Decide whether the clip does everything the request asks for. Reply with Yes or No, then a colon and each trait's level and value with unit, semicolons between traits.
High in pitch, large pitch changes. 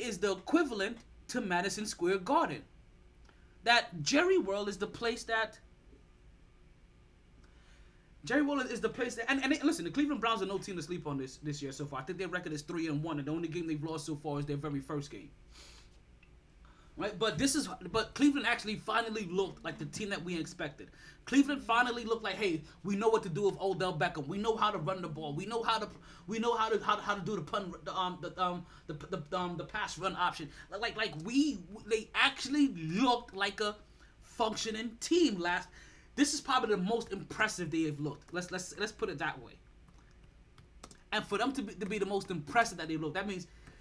Yes: high, 195 Hz; wide, 5.8 semitones